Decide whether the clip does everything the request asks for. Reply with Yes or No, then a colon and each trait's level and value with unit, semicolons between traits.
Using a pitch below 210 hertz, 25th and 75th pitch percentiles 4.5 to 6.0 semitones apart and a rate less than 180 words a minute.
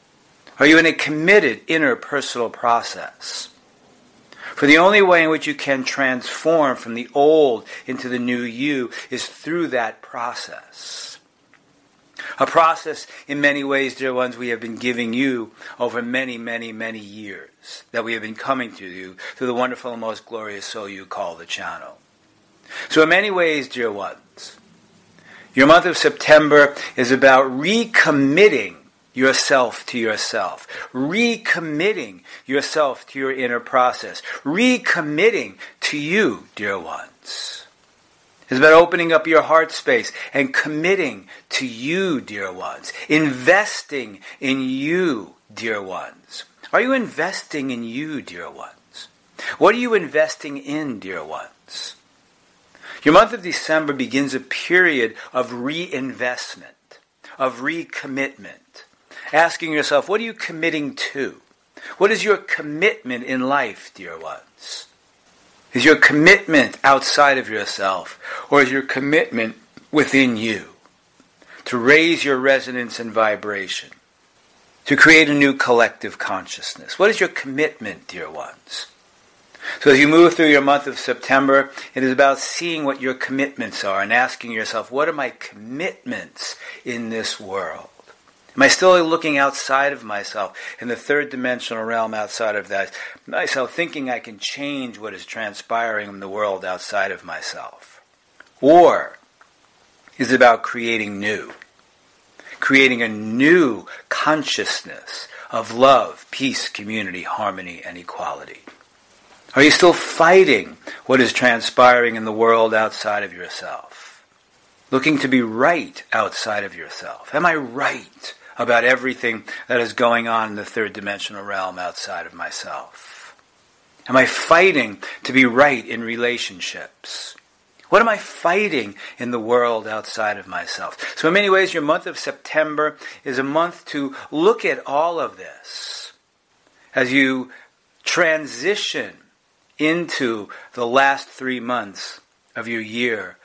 Yes: low, 135 Hz; average, 4.8 semitones; average, 140 wpm